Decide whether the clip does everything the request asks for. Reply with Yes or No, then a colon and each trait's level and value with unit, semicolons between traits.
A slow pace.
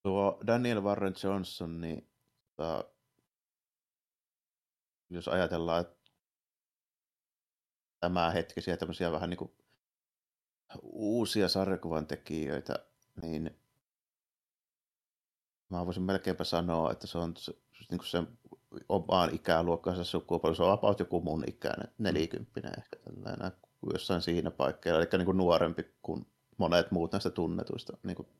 No: average, 110 wpm